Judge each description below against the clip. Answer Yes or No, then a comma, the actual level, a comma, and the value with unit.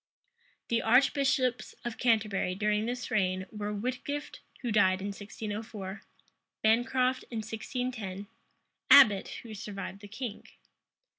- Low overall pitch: No, high, 220 Hz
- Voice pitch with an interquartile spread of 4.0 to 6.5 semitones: No, average, 3.4 semitones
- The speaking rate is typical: No, slow, 115 wpm